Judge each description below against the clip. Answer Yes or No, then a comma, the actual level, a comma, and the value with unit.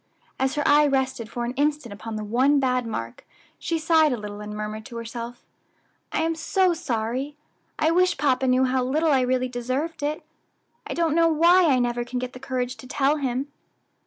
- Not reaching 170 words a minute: No, average, 200 wpm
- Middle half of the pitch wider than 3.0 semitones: Yes, average, 3.8 semitones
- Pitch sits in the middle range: No, very high, 260 Hz